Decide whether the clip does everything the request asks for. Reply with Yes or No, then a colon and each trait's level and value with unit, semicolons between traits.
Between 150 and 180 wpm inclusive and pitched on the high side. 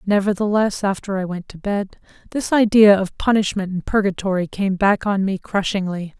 Yes: average, 165 wpm; high, 195 Hz